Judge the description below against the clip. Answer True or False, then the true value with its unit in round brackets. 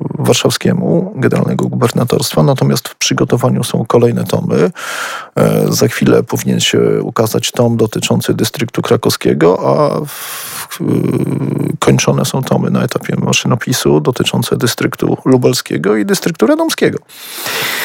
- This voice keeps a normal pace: False (105 wpm)